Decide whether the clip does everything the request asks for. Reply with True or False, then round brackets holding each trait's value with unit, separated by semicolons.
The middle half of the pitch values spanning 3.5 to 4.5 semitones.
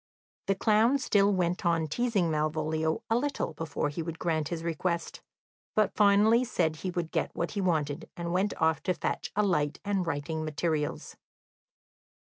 True (4.2 semitones)